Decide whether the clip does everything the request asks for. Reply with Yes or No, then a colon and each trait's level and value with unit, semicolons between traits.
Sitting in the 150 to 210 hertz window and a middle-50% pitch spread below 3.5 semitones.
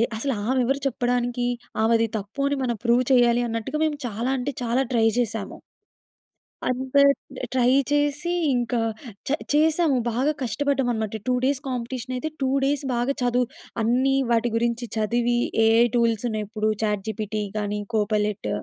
No: high, 240 Hz; average, 2.8 semitones